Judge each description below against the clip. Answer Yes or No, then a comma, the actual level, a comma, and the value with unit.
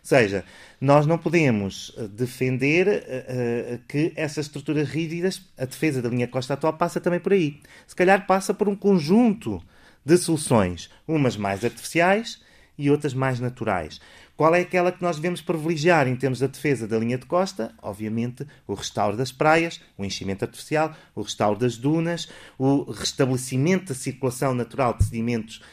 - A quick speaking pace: No, average, 165 wpm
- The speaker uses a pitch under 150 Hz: Yes, medium, 140 Hz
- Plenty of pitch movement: Yes, wide, 5.9 semitones